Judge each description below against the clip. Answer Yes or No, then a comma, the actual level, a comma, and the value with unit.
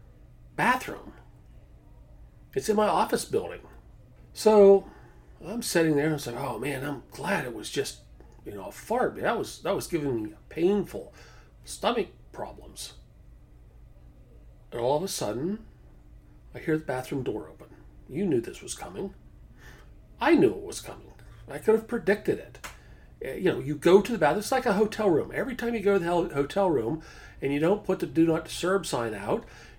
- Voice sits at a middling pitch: Yes, medium, 160 Hz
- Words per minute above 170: Yes, average, 185 wpm